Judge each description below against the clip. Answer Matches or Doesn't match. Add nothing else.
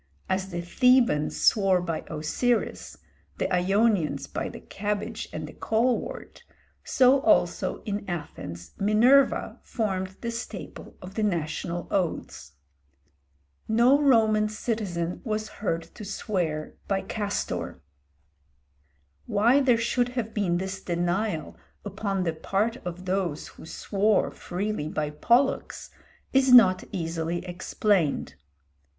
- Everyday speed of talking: Doesn't match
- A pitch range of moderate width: Matches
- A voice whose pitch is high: Matches